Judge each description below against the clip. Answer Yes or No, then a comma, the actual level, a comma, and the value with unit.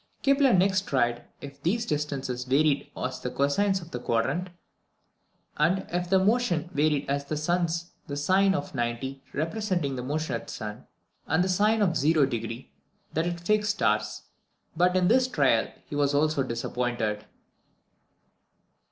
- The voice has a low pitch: No, medium, 150 Hz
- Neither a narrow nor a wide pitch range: No, wide, 5.7 semitones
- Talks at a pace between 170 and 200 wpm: No, average, 155 wpm